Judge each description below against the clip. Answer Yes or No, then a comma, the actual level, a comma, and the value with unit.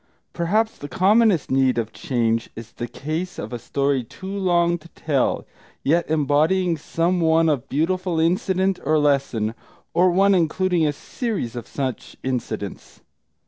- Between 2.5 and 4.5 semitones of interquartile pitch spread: No, wide, 5.4 semitones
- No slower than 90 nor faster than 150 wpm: Yes, average, 145 wpm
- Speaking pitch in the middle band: Yes, medium, 160 Hz